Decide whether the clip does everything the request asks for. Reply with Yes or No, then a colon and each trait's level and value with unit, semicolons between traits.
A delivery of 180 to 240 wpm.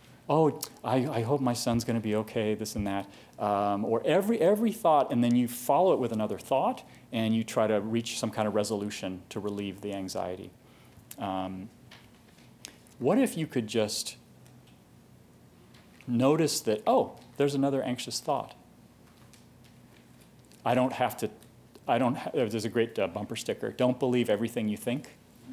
No: average, 160 wpm